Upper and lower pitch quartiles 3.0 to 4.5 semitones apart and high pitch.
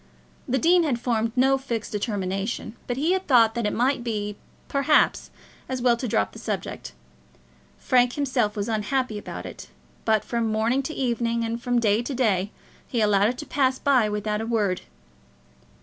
Yes: average, 3.4 semitones; high, 235 Hz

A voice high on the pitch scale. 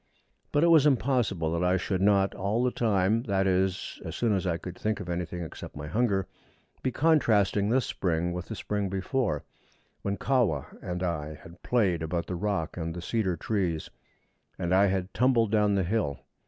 No: very low, 95 Hz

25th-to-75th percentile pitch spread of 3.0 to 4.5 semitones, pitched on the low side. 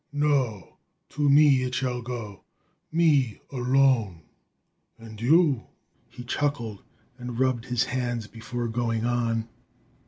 No: narrow, 2.6 semitones; low, 120 Hz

